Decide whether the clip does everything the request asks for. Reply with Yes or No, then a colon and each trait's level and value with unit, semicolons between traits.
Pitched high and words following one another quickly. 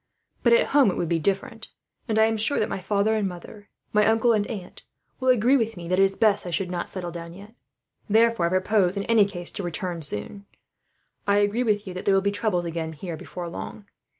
Yes: high, 200 Hz; fast, 230 wpm